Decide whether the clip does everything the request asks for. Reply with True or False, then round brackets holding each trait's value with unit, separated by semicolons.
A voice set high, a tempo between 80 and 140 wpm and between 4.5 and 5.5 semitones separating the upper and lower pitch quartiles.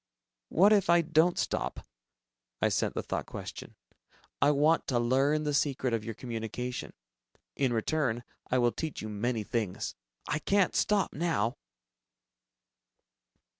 False (135 Hz; 135 wpm; 5.1 semitones)